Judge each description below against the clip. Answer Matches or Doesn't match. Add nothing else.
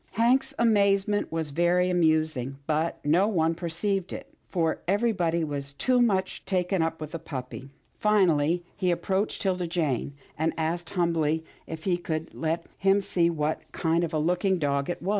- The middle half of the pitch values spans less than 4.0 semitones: Matches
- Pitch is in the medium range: Matches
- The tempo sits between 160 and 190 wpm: Matches